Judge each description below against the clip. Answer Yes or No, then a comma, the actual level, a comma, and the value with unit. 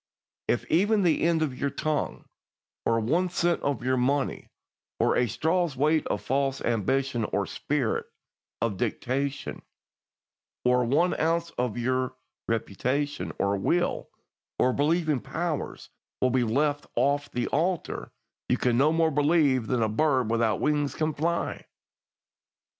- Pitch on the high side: No, medium, 140 Hz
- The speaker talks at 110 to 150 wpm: Yes, slow, 135 wpm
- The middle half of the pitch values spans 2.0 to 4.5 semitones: Yes, average, 4.2 semitones